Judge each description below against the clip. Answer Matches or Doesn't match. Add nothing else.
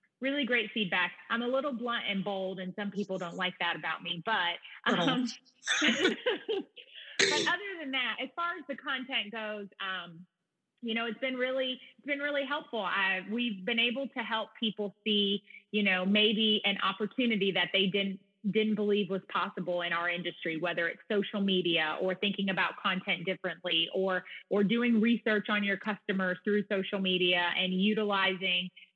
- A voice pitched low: Doesn't match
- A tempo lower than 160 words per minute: Doesn't match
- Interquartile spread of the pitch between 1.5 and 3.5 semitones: Doesn't match